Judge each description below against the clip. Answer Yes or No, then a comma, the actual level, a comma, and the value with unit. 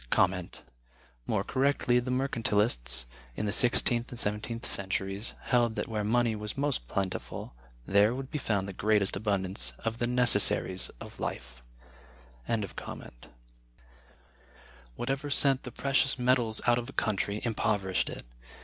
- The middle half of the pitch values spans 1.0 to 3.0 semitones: No, average, 4.1 semitones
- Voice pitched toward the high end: No, low, 110 Hz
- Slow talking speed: Yes, slow, 130 wpm